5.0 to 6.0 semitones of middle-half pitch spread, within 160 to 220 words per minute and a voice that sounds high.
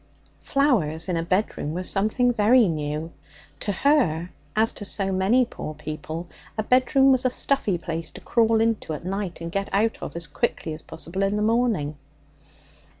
Yes: wide, 5.6 semitones; average, 175 wpm; high, 195 Hz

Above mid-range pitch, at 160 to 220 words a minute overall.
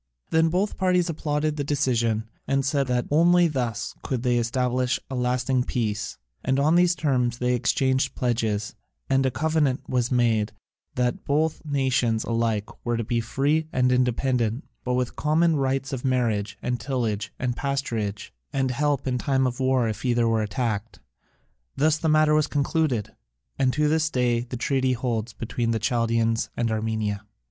No: low, 125 Hz; average, 165 wpm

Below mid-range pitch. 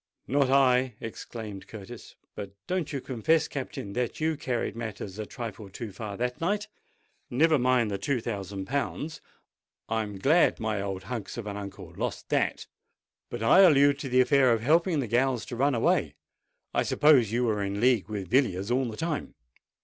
Yes: low, 120 Hz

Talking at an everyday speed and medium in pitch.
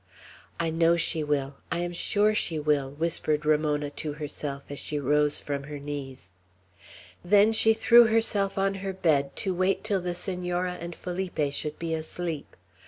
Yes: average, 170 wpm; medium, 165 Hz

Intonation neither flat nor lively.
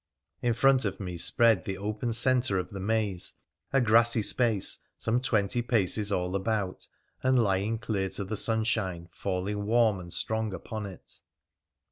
Yes: average, 3.3 semitones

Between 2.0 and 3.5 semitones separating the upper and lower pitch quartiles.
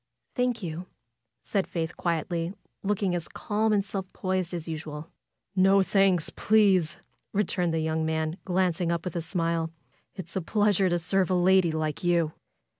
Yes: average, 2.9 semitones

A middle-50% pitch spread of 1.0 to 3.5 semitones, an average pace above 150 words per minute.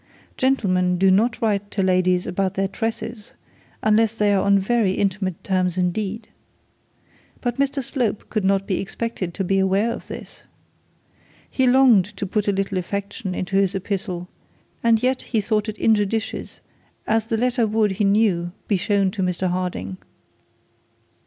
Yes: average, 3.0 semitones; average, 160 wpm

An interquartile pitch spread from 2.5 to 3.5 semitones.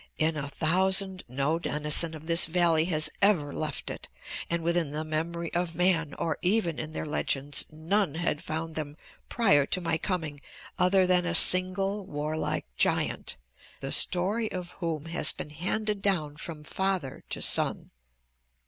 Yes: average, 3.0 semitones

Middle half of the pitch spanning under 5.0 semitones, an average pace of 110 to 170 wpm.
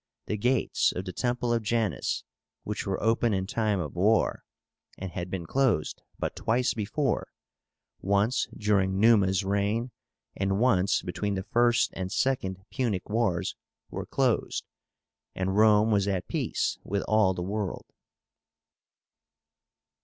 Yes: average, 3.3 semitones; slow, 135 wpm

